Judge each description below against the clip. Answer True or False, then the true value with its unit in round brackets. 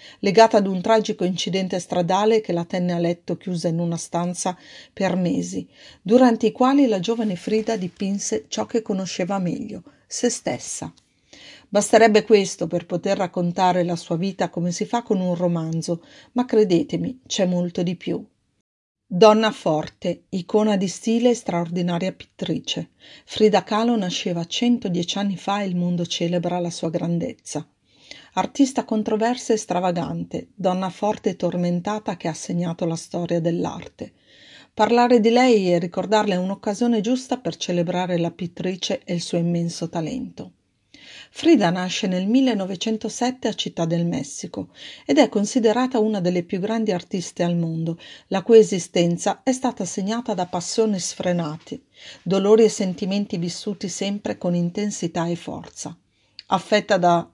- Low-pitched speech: False (190 Hz)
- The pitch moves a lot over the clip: False (3.8 semitones)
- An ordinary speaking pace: True (145 wpm)